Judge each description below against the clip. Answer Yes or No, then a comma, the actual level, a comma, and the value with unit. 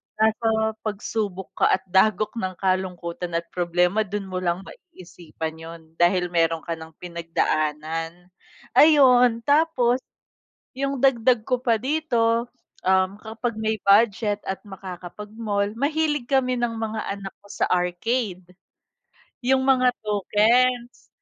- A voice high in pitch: Yes, high, 210 Hz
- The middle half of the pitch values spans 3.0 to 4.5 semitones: No, average, 5.2 semitones